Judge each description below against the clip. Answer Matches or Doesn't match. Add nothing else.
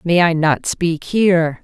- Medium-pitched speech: Matches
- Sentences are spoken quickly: Doesn't match